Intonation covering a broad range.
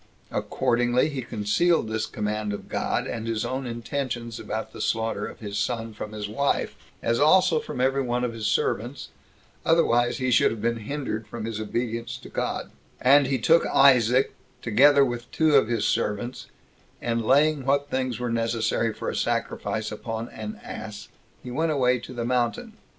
No: average, 3.1 semitones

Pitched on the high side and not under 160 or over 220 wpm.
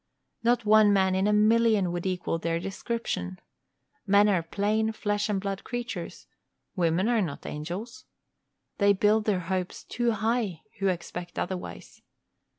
No: high, 200 Hz; average, 145 wpm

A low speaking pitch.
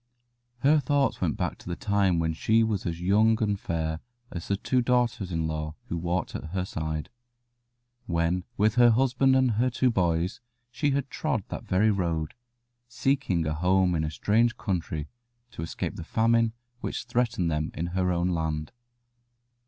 Yes: very low, 95 Hz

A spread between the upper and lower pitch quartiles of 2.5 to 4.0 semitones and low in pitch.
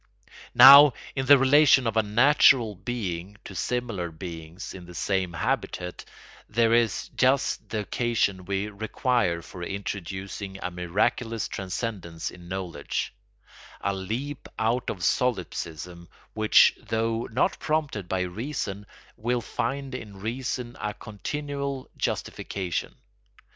No: average, 5.1 semitones; low, 105 Hz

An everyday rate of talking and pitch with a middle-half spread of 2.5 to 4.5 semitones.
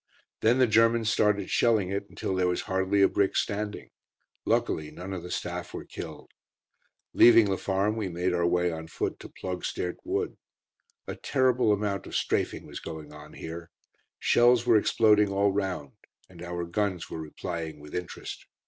Yes: average, 170 wpm; average, 3.4 semitones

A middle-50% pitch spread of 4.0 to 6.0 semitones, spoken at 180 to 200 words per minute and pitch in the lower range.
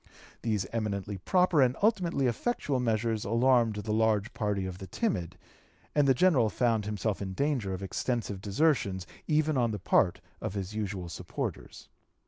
No: average, 4.9 semitones; average, 155 wpm; low, 110 Hz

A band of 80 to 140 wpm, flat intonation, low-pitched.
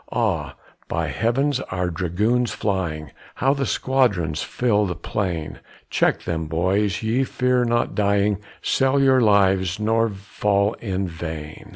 No: slow, 135 wpm; average, 5.0 semitones; low, 100 Hz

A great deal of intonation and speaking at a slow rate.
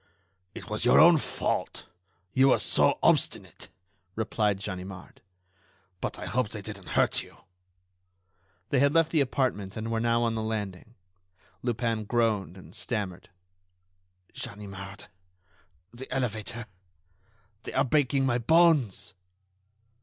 No: average, 3.8 semitones; slow, 125 wpm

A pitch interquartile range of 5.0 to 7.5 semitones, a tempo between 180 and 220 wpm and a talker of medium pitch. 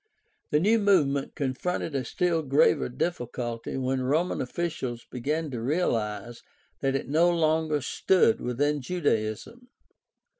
No: wide, 5.4 semitones; slow, 135 wpm; medium, 145 Hz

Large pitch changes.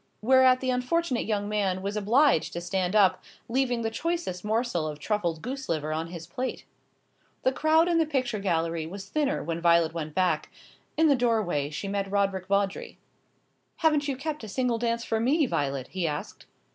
Yes: wide, 7.0 semitones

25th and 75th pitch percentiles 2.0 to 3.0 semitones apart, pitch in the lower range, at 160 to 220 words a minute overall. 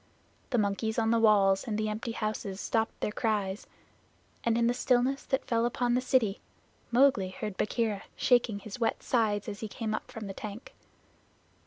No: narrow, 2.5 semitones; high, 220 Hz; average, 180 wpm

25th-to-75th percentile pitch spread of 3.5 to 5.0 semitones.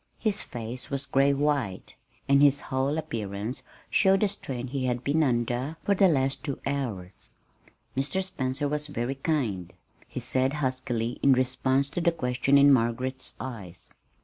No: average, 2.9 semitones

